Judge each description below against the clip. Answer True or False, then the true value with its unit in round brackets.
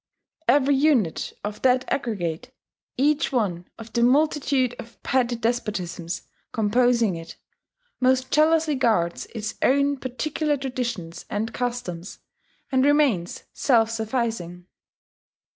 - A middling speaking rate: False (110 wpm)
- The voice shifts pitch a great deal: False (4.3 semitones)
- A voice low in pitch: False (240 Hz)